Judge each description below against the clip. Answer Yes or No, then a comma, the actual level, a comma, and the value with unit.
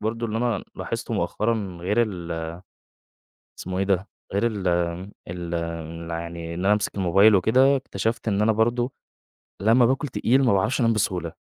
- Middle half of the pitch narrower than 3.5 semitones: No, average, 4.8 semitones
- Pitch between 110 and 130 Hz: No, low, 100 Hz